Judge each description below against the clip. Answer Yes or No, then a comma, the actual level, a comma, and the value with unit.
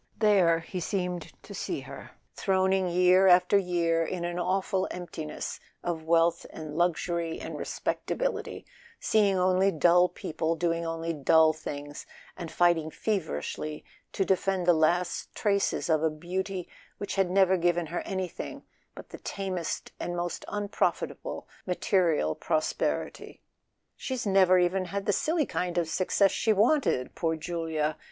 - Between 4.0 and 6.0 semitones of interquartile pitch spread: No, narrow, 2.5 semitones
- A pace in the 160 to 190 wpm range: No, average, 140 wpm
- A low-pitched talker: No, medium, 175 Hz